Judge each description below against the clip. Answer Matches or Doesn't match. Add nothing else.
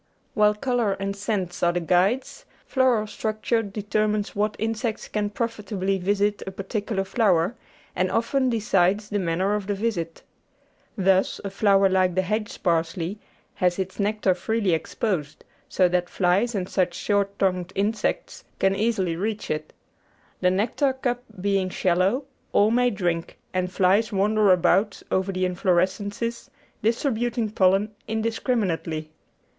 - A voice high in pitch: Matches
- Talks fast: Doesn't match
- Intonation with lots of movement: Doesn't match